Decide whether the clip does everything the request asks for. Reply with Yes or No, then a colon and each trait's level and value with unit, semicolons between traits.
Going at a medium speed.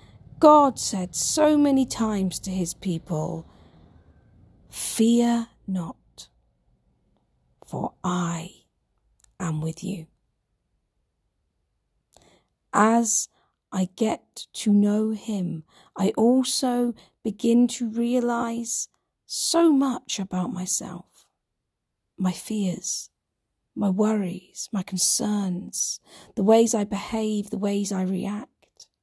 No: slow, 90 wpm